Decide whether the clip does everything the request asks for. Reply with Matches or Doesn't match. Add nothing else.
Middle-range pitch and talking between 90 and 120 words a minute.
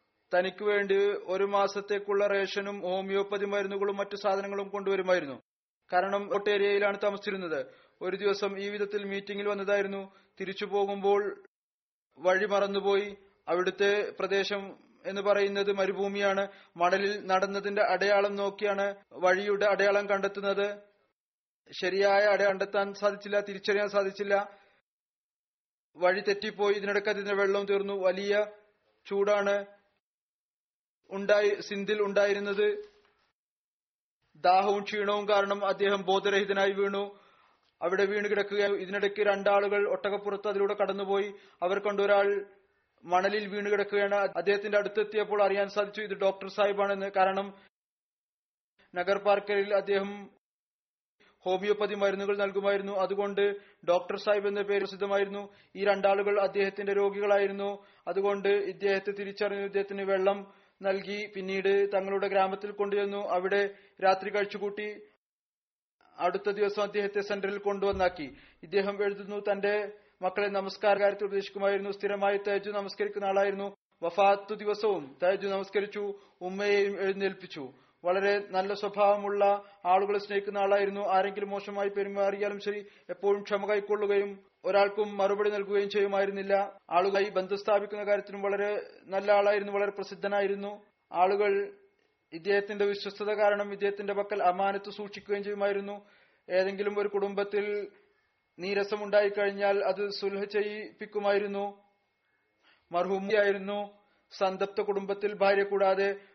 Doesn't match